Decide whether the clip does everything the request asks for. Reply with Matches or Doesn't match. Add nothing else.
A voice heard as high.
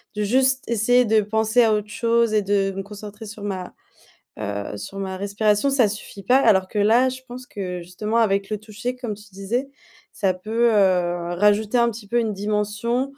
Matches